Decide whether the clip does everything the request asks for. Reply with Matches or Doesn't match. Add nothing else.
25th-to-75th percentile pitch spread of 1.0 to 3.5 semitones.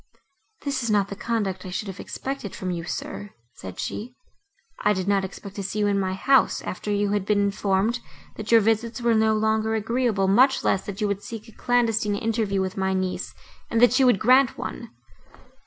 Matches